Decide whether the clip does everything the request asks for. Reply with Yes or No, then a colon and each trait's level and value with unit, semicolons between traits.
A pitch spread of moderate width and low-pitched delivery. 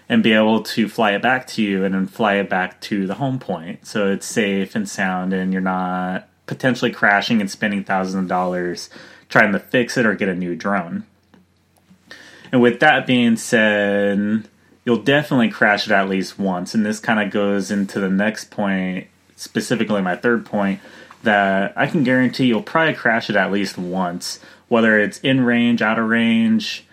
Yes: average, 3.2 semitones; low, 100 Hz